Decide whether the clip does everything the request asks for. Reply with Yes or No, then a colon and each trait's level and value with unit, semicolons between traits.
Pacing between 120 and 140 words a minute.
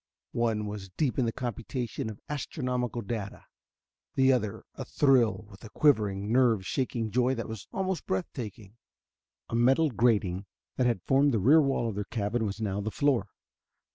No: average, 170 wpm